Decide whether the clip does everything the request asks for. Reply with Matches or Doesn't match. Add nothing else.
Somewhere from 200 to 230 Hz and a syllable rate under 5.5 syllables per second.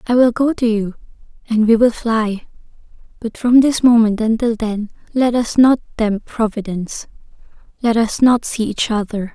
Matches